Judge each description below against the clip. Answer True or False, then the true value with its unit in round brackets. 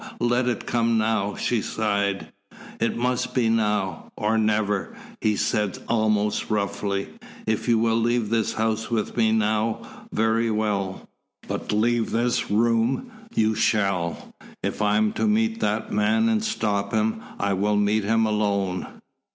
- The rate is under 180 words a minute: True (150 wpm)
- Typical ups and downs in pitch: False (1.9 semitones)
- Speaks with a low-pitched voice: True (110 Hz)